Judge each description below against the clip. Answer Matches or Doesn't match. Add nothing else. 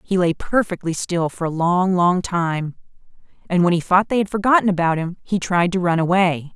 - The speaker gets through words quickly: Matches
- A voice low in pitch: Doesn't match